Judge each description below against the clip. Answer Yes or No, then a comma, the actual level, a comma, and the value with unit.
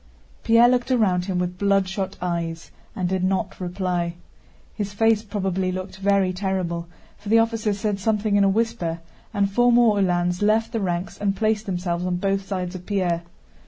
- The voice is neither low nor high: No, high, 195 Hz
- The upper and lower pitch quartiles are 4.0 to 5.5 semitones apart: No, average, 2.8 semitones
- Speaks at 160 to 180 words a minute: Yes, average, 175 wpm